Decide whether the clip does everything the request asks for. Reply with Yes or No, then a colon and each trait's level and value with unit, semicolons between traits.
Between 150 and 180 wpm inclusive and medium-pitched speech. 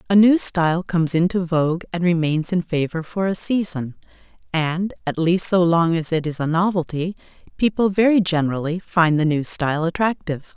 Yes: average, 175 wpm; medium, 170 Hz